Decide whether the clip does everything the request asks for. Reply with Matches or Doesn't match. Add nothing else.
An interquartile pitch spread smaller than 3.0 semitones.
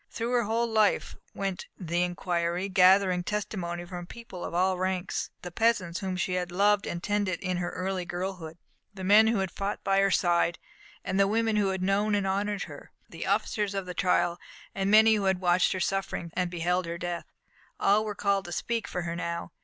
Matches